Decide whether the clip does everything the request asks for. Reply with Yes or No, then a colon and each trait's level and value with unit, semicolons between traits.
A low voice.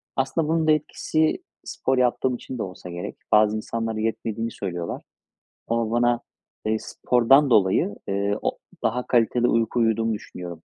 Yes: low, 115 Hz